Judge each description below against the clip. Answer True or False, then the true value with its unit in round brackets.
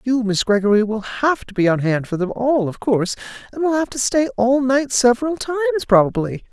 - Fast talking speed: True (220 wpm)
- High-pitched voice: True (240 Hz)